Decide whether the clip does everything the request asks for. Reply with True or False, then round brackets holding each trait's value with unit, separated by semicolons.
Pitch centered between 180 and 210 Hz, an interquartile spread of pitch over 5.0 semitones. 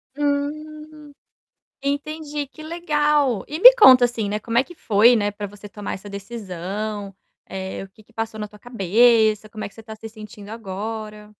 False (225 Hz; 5.6 semitones)